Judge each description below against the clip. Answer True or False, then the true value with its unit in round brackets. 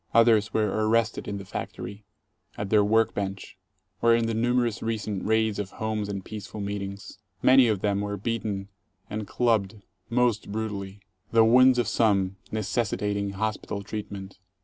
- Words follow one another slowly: False (150 wpm)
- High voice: False (105 Hz)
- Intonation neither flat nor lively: False (2.0 semitones)